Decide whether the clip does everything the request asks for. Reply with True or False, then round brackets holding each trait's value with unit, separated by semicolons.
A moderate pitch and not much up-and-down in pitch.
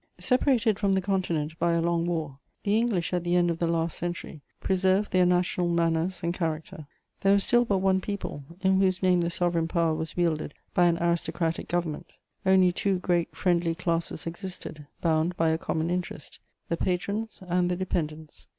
True (175 Hz; 2.2 semitones)